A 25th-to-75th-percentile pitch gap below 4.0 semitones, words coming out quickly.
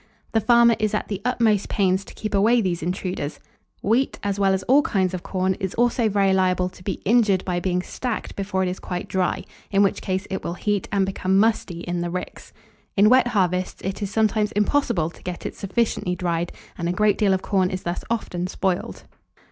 Yes: average, 2.7 semitones; fast, 210 wpm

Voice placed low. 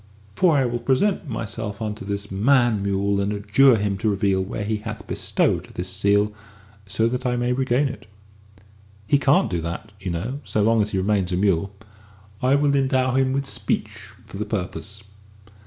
Yes: low, 105 Hz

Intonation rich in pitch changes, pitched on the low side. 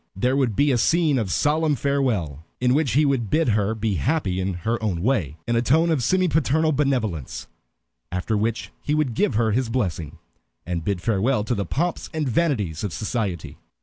Yes: wide, 6.3 semitones; low, 115 Hz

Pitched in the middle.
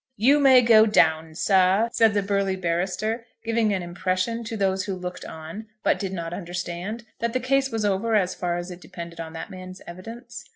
No: high, 195 Hz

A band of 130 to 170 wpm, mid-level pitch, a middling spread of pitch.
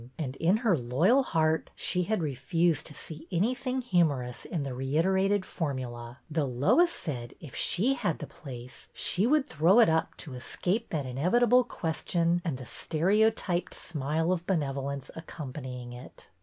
No: average, 160 wpm; medium, 160 Hz; wide, 5.8 semitones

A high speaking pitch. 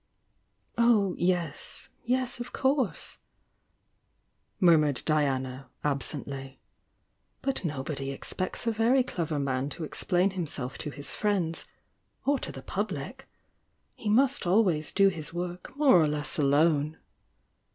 No: medium, 170 Hz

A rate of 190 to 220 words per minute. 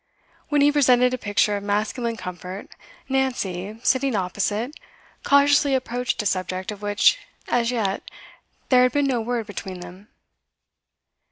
No: average, 140 wpm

